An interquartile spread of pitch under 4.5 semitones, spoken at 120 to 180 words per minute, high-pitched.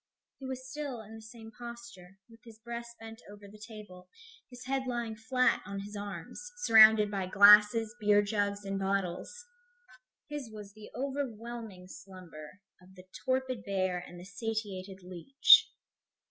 Yes: average, 3.3 semitones; average, 150 wpm; high, 215 Hz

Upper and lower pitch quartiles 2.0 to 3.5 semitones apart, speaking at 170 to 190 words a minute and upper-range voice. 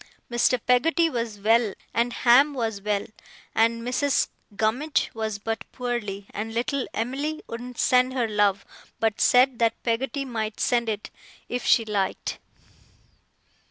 No: narrow, 2.5 semitones; slow, 135 wpm; high, 235 Hz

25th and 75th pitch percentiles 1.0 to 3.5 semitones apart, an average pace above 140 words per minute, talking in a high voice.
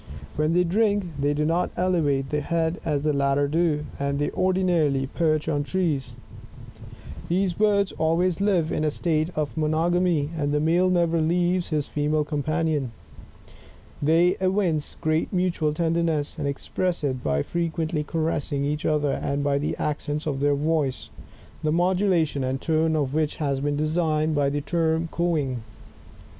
No: average, 2.9 semitones; average, 155 wpm; medium, 155 Hz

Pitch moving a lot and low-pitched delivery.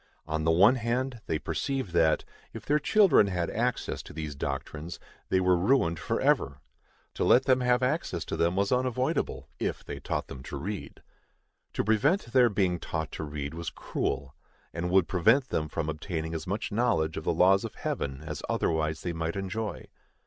Yes: wide, 7.1 semitones; very low, 90 Hz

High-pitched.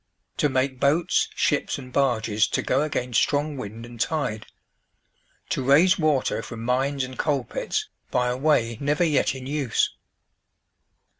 No: low, 135 Hz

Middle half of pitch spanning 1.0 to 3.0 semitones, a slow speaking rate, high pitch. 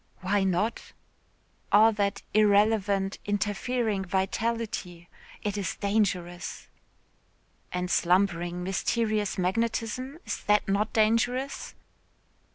Yes: average, 2.7 semitones; slow, 85 wpm; high, 205 Hz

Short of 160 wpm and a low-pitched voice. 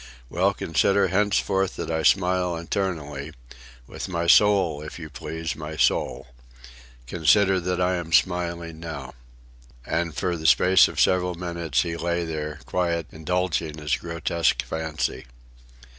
Yes: slow, 135 wpm; very low, 85 Hz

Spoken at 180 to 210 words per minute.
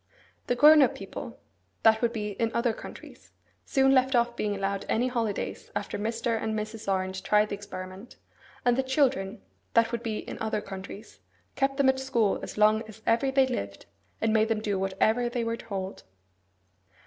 Yes: average, 185 wpm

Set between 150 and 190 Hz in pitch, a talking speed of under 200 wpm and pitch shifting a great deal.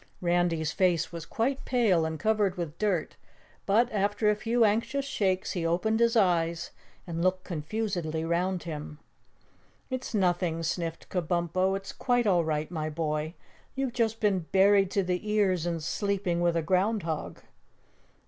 No: medium, 185 Hz; average, 155 wpm; average, 4.0 semitones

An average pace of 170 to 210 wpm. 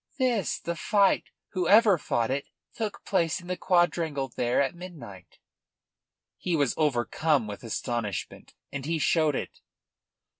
No: slow, 135 wpm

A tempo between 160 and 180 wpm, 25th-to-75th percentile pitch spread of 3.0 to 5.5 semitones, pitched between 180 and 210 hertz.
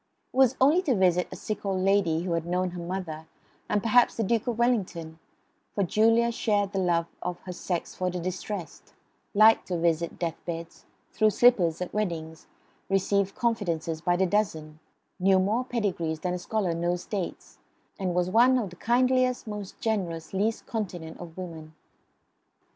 Yes: average, 170 wpm; average, 4.1 semitones; medium, 185 Hz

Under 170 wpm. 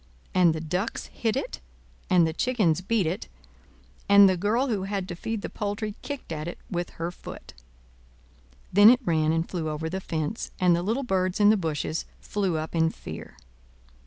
No: average, 190 wpm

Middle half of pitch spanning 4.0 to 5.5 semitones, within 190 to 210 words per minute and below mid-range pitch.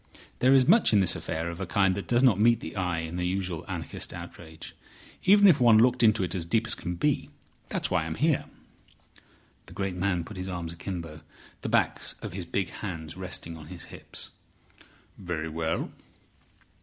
Yes: average, 4.4 semitones; average, 195 wpm; very low, 90 Hz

